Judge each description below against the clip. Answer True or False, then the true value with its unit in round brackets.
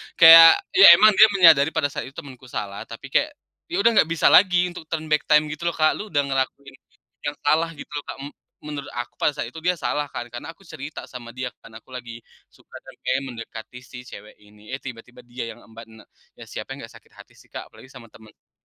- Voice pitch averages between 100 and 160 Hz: True (140 Hz)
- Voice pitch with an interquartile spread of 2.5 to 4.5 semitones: False (4.9 semitones)